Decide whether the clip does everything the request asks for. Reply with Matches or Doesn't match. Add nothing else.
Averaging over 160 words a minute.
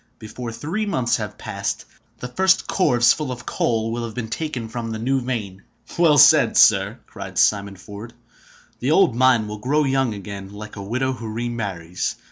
Matches